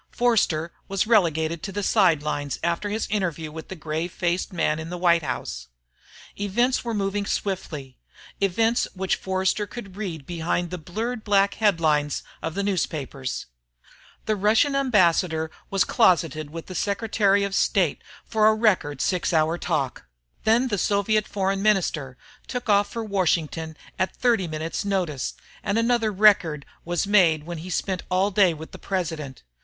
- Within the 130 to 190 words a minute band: Yes, average, 155 wpm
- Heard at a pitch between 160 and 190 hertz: Yes, medium, 185 Hz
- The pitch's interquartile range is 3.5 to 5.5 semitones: Yes, average, 4.4 semitones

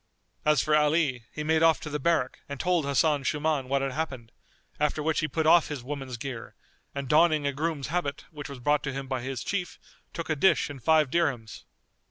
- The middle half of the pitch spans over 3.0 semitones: No, average, 2.7 semitones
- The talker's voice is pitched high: No, medium, 145 Hz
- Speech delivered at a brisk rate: Yes, fast, 215 wpm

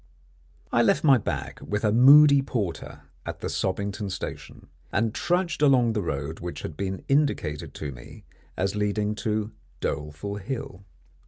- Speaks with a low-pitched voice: Yes, low, 105 Hz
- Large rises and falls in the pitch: Yes, wide, 6.0 semitones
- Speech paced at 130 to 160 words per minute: Yes, average, 150 wpm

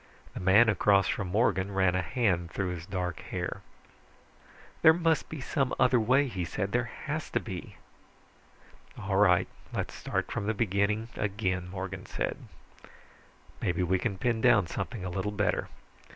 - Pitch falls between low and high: No, low, 100 Hz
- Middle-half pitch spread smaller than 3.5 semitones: No, average, 3.8 semitones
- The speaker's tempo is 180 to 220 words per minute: No, average, 160 wpm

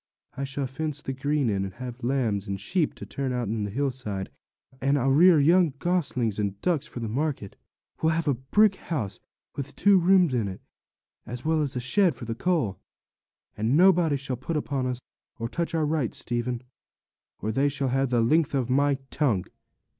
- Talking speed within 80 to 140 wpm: No, average, 195 wpm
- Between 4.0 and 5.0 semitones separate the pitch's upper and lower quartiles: Yes, average, 4.7 semitones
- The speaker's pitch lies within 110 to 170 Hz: Yes, low, 135 Hz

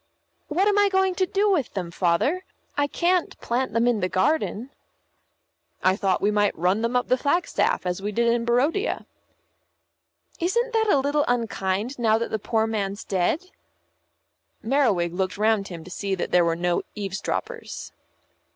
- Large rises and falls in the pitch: Yes, wide, 7.5 semitones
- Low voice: No, high, 230 Hz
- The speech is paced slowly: No, average, 170 wpm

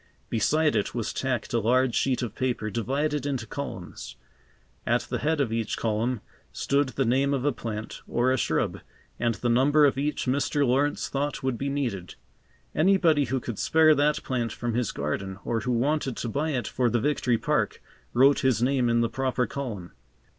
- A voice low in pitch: Yes, low, 130 Hz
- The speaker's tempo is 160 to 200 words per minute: Yes, average, 190 wpm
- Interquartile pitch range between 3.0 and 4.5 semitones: Yes, average, 3.4 semitones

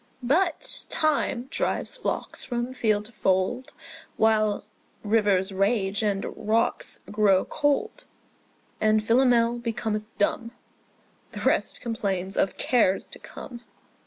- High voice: Yes, high, 220 Hz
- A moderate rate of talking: No, slow, 110 wpm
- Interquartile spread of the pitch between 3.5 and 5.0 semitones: No, average, 3.0 semitones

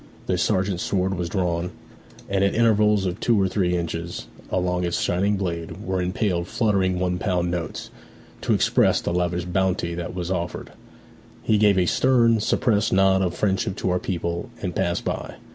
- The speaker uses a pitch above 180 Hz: No, very low, 90 Hz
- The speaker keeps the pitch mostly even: Yes, narrow, 2.1 semitones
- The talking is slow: No, average, 175 wpm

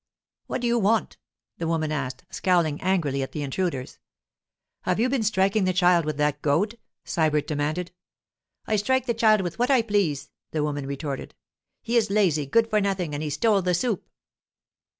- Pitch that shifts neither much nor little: No, wide, 6.1 semitones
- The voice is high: No, medium, 180 Hz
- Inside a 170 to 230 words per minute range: Yes, average, 185 wpm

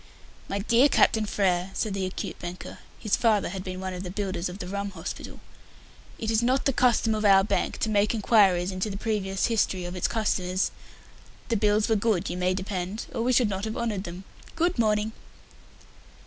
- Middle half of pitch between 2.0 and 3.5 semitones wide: Yes, average, 3.0 semitones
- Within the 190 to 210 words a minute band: Yes, average, 200 wpm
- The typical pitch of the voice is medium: No, high, 200 Hz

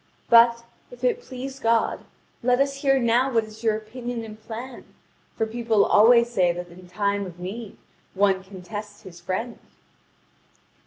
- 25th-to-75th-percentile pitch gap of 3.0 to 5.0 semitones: Yes, average, 3.3 semitones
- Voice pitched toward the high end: Yes, high, 225 Hz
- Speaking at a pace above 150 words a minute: Yes, average, 160 wpm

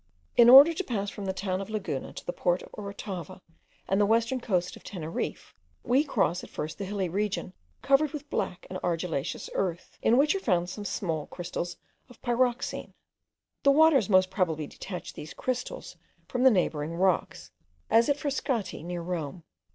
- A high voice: Yes, high, 195 Hz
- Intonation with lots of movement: Yes, wide, 5.8 semitones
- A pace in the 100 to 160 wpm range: No, average, 175 wpm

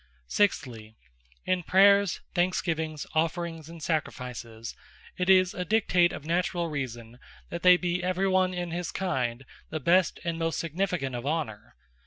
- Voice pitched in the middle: Yes, medium, 170 Hz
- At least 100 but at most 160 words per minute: Yes, average, 145 wpm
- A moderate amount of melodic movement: Yes, average, 4.2 semitones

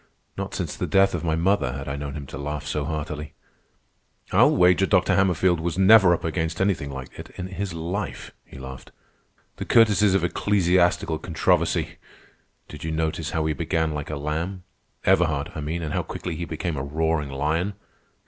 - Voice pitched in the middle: No, very low, 80 Hz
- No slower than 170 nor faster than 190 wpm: Yes, average, 180 wpm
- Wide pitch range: No, average, 3.4 semitones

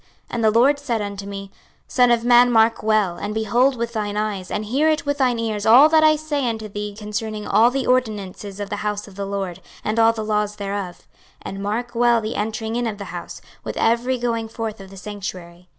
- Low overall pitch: No, high, 220 Hz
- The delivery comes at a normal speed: No, fast, 225 wpm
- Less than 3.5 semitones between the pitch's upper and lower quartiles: Yes, average, 2.8 semitones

